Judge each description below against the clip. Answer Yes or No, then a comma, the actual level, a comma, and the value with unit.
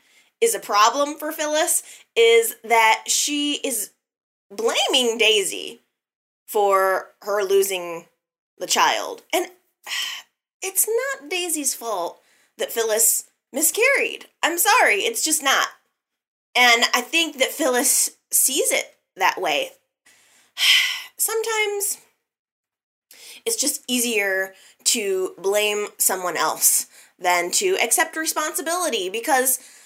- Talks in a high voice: Yes, very high, 310 Hz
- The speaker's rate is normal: No, slow, 100 wpm